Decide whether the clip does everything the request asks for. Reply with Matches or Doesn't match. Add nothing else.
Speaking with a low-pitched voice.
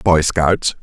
Matches